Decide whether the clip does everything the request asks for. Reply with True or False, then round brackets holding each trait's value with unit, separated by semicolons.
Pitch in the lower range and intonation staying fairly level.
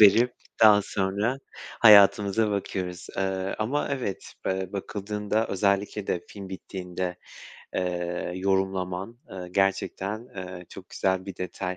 True (95 Hz; 2.0 semitones)